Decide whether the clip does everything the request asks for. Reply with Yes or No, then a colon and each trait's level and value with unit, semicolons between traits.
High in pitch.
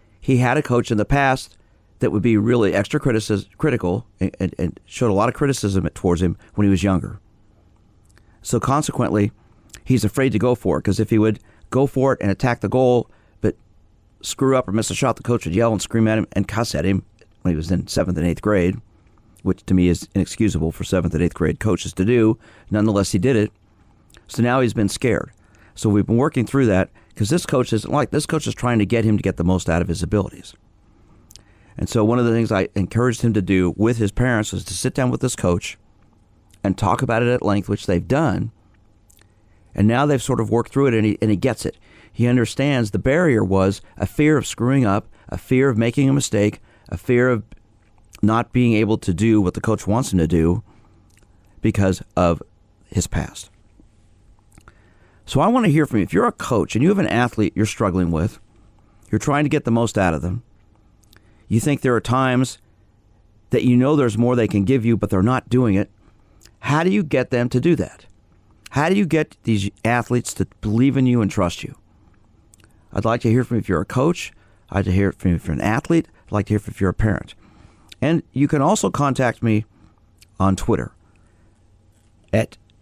No: low, 105 Hz